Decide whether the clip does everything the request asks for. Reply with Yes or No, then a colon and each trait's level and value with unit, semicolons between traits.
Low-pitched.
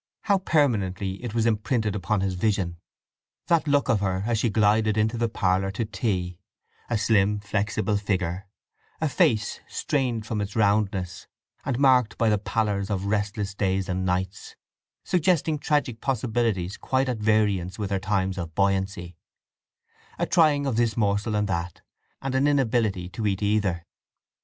Yes: low, 105 Hz